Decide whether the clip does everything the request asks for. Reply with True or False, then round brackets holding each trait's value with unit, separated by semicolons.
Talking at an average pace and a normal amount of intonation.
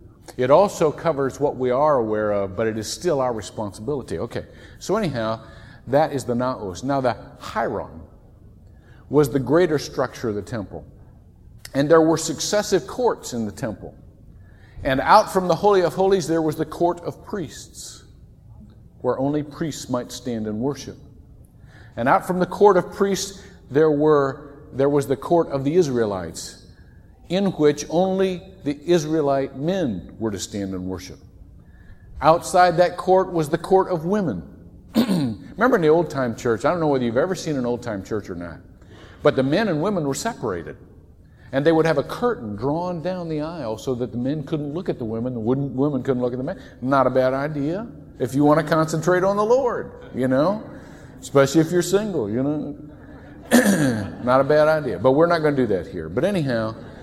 False (190 wpm; 6.3 semitones)